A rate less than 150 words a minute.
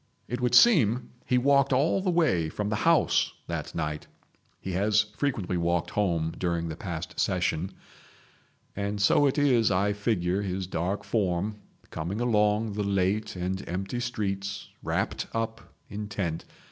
Yes: average, 140 wpm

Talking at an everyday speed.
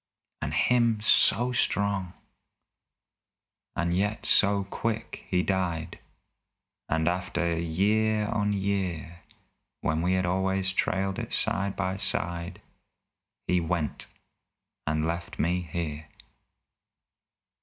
No: slow, 100 wpm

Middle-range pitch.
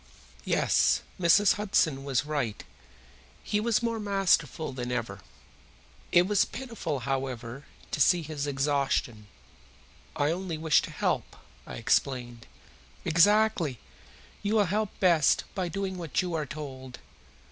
Yes: medium, 155 Hz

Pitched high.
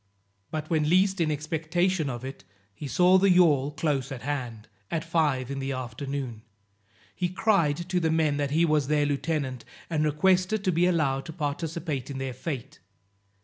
No: medium, 150 Hz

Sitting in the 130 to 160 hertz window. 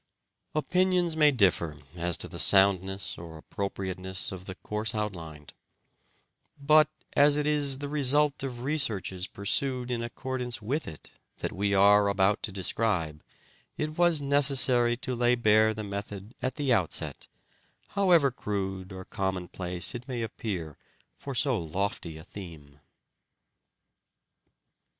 No: low, 105 Hz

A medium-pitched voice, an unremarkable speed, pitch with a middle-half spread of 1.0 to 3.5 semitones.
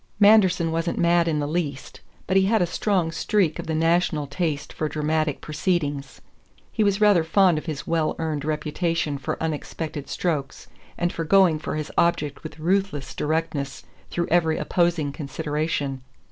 Yes: medium, 160 Hz; average, 160 wpm; average, 2.7 semitones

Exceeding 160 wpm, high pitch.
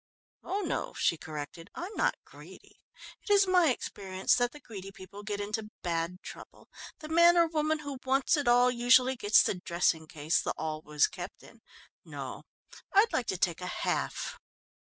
Yes: average, 180 wpm; high, 225 Hz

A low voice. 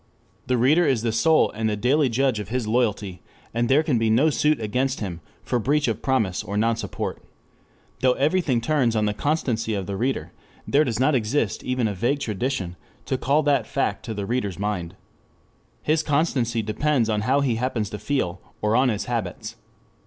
Yes: low, 120 Hz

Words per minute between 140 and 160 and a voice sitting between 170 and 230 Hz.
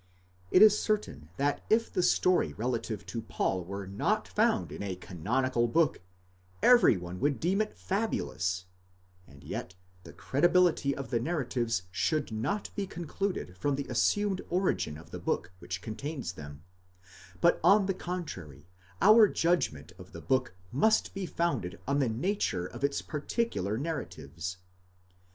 No: average, 150 wpm; low, 135 Hz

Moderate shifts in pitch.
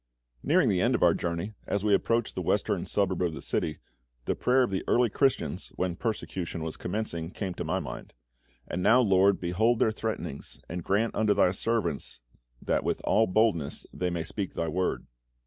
Yes: average, 4.2 semitones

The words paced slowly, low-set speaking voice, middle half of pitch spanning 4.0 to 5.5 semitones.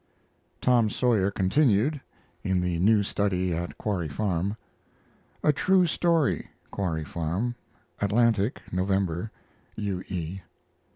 Yes: slow, 105 wpm; low, 100 Hz; average, 4.5 semitones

